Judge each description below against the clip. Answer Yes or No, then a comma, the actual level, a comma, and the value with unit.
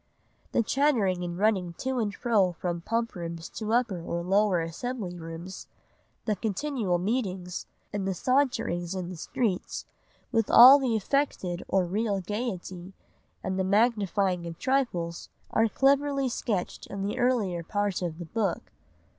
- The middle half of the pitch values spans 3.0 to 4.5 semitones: No, average, 4.9 semitones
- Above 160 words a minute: No, average, 145 wpm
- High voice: Yes, high, 195 Hz